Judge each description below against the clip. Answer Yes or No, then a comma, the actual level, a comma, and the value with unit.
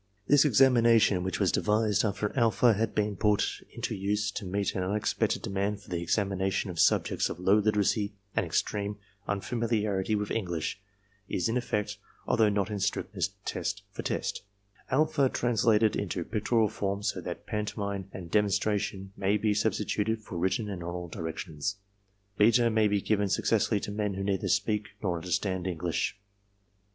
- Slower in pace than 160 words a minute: No, average, 170 wpm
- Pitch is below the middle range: Yes, low, 105 Hz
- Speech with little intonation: Yes, narrow, 2.0 semitones